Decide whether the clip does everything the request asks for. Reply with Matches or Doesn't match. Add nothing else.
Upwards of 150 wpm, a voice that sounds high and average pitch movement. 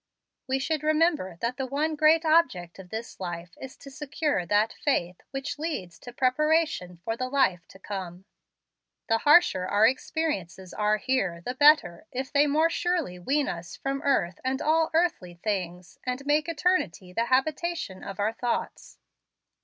Doesn't match